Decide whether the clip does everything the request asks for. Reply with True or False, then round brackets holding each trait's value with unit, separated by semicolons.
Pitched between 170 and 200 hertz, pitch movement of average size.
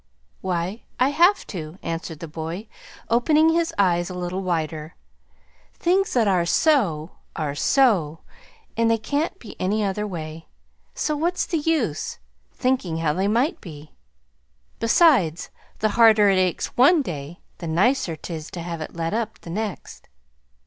False (190 Hz; 7.2 semitones)